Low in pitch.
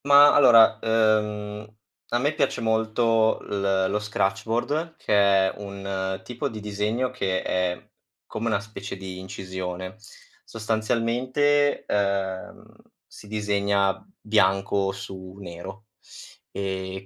Yes: low, 105 Hz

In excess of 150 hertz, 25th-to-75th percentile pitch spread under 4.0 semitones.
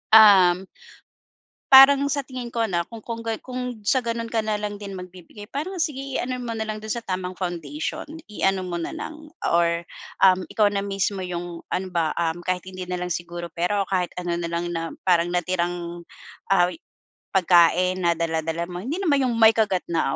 No: medium, 185 Hz; average, 4.4 semitones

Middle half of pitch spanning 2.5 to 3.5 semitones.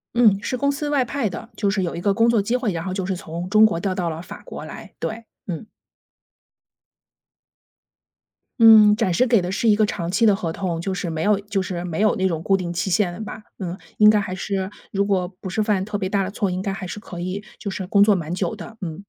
Yes: average, 3.0 semitones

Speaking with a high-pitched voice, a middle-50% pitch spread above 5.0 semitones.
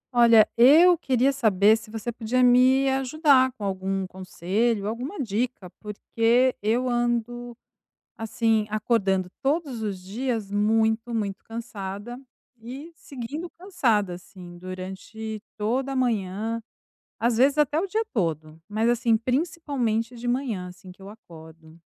No: high, 230 Hz; average, 4.1 semitones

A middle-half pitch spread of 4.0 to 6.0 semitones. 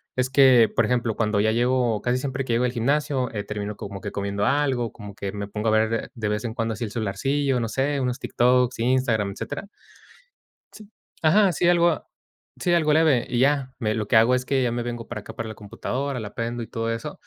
No: average, 3.4 semitones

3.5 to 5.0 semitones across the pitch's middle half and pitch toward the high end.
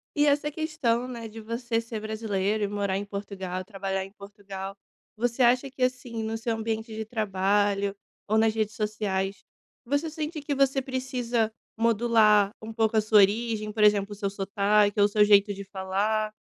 No: average, 2.7 semitones; high, 215 Hz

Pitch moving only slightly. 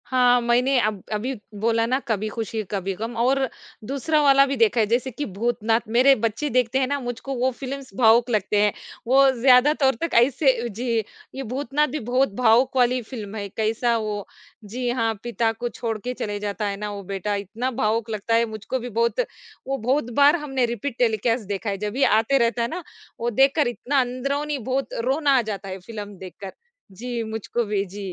No: average, 3.4 semitones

